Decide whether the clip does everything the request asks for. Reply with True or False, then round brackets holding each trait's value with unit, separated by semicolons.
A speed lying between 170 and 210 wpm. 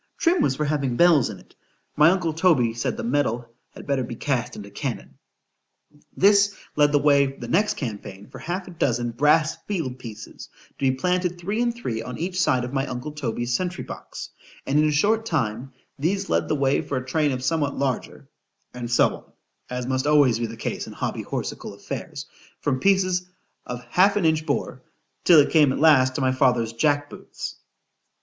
True (190 wpm)